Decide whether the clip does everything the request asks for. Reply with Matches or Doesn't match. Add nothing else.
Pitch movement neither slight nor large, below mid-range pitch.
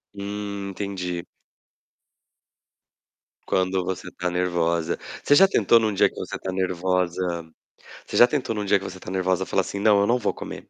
Doesn't match